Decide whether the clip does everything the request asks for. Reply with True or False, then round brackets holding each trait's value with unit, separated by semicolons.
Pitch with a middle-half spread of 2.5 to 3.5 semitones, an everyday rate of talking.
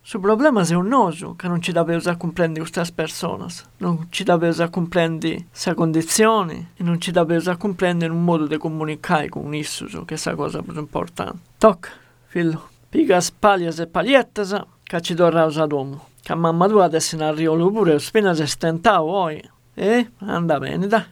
False (2.9 semitones; 215 wpm)